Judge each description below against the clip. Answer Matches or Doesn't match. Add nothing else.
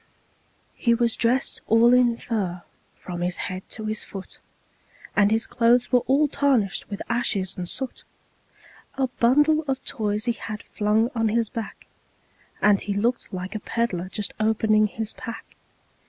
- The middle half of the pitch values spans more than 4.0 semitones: Doesn't match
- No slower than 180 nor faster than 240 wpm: Doesn't match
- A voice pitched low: Doesn't match